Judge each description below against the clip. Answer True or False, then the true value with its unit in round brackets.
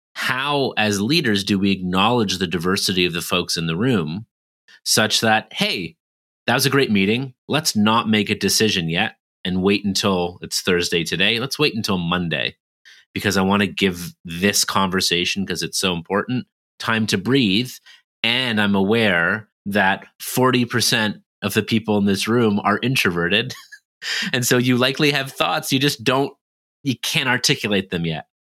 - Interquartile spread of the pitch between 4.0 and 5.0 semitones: True (4.6 semitones)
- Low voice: True (105 Hz)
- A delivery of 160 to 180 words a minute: True (165 wpm)